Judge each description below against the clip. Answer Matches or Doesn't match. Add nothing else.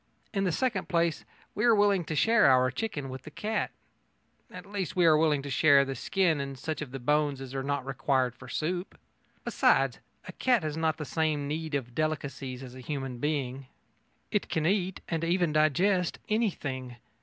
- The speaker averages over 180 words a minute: Matches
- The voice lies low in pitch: Doesn't match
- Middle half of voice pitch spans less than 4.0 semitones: Doesn't match